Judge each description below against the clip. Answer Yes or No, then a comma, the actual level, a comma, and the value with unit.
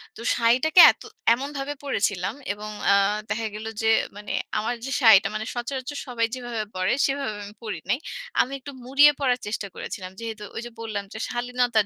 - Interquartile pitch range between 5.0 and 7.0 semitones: No, average, 3.4 semitones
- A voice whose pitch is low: No, high, 235 Hz